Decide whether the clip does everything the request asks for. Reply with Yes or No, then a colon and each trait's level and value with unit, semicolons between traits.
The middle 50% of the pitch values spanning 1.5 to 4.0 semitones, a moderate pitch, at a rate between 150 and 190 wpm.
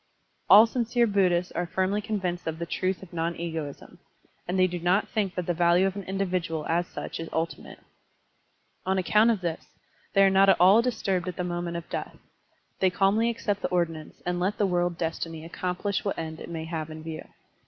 No: narrow, 2.6 semitones; medium, 180 Hz; fast, 205 wpm